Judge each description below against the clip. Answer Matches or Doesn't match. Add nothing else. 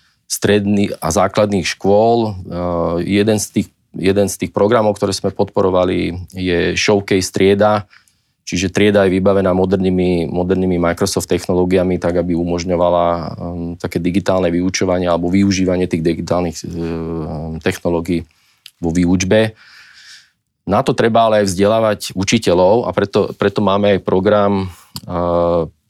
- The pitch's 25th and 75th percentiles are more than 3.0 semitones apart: Doesn't match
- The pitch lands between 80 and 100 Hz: Matches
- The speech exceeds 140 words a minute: Doesn't match